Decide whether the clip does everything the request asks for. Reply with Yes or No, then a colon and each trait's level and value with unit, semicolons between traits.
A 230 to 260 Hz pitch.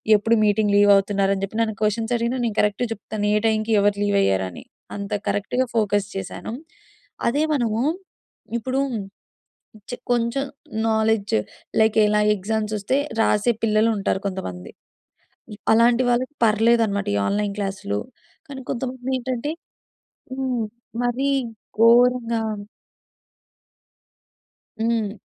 No: high, 220 Hz